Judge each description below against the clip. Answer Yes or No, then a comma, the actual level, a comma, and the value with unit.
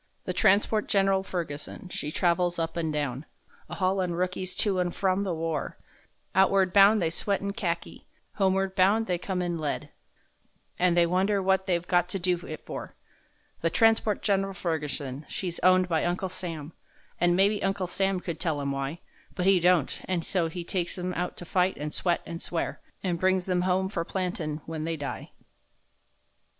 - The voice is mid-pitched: Yes, medium, 180 Hz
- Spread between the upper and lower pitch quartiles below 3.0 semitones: Yes, narrow, 2.4 semitones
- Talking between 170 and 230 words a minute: Yes, average, 180 wpm